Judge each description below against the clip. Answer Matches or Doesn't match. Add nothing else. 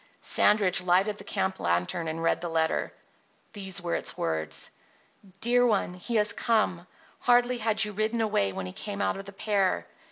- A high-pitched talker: Matches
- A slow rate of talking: Doesn't match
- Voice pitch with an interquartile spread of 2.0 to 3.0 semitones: Doesn't match